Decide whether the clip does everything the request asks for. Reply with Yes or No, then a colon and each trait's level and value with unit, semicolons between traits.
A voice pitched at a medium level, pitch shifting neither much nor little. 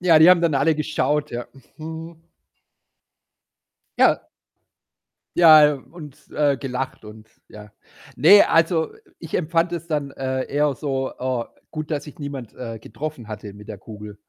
Yes: medium, 145 Hz; average, 4.4 semitones